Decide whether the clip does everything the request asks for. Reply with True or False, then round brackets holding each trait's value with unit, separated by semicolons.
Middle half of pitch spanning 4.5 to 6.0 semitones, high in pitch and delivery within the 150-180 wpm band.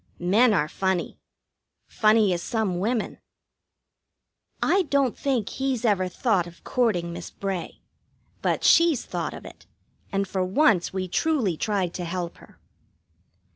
False (5.1 semitones; 195 Hz; 135 wpm)